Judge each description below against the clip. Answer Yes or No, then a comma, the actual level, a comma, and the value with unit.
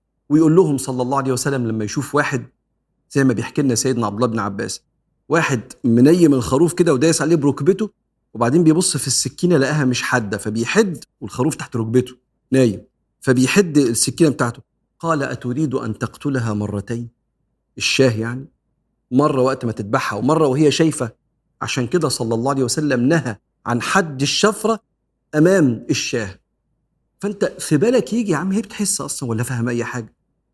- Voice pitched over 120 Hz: Yes, low, 135 Hz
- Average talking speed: No, fast, 155 wpm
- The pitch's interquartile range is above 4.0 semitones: Yes, average, 4.8 semitones